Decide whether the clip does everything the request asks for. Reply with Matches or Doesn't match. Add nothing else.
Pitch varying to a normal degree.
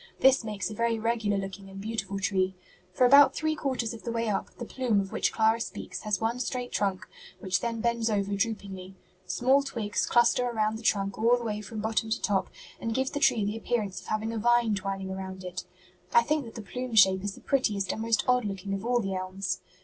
Matches